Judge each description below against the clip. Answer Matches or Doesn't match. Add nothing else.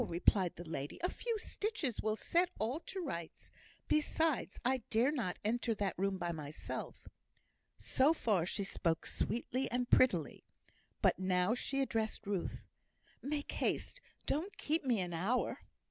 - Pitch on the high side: Matches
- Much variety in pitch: Matches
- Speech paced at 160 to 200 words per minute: Doesn't match